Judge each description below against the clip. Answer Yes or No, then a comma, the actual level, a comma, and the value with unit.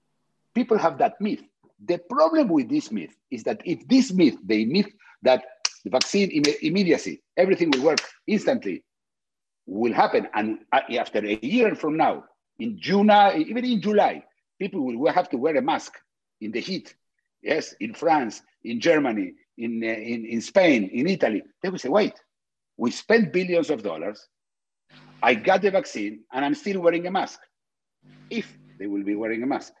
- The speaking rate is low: No, average, 170 wpm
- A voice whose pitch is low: No, high, 190 Hz